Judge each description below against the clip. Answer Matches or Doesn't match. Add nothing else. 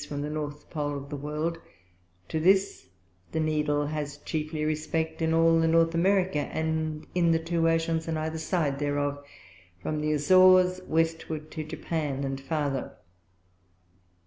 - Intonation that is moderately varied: Doesn't match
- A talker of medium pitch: Matches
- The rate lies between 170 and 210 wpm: Doesn't match